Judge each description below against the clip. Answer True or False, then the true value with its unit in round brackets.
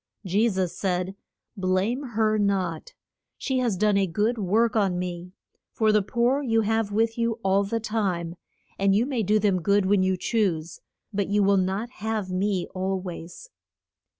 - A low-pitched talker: False (200 Hz)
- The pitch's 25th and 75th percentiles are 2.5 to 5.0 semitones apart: True (3.0 semitones)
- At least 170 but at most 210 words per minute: True (175 wpm)